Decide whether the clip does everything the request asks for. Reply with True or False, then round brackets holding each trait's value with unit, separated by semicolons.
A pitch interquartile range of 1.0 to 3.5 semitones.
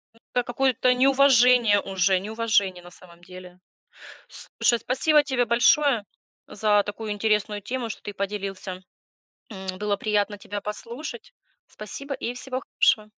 False (3.9 semitones)